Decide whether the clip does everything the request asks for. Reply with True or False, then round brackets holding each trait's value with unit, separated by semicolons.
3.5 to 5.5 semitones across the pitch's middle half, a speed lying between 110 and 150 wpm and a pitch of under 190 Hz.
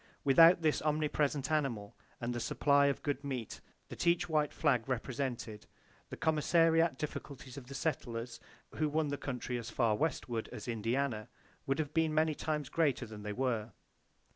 False (4.3 semitones; 165 wpm; 140 Hz)